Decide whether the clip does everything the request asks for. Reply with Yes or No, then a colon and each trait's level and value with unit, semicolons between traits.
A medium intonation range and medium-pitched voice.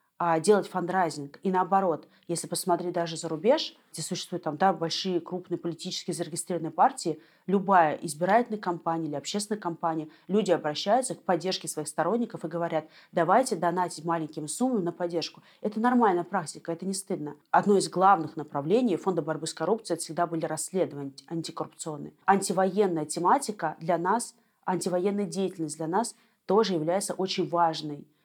Yes: average, 3.0 semitones; medium, 175 Hz